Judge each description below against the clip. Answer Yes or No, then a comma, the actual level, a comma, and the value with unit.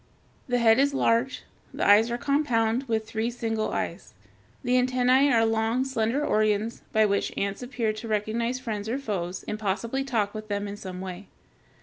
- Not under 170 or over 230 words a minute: Yes, average, 180 wpm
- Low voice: No, high, 225 Hz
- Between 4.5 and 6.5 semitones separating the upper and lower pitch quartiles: No, average, 2.7 semitones